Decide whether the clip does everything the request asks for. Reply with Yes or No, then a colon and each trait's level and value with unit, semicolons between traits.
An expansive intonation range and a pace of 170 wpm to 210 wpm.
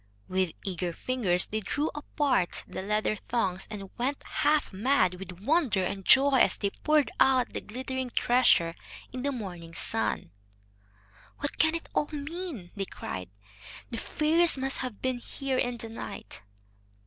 No: wide, 6.6 semitones; average, 155 wpm